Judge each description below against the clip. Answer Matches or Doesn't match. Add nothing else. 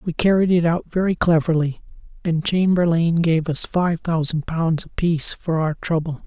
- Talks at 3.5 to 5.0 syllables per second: Matches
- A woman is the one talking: Doesn't match